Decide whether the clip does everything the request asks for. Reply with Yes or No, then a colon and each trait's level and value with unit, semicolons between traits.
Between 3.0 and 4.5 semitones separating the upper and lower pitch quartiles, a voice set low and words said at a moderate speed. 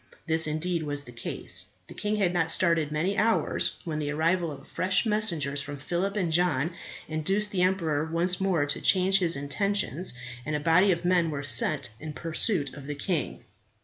No: average, 3.9 semitones; medium, 165 Hz; average, 185 wpm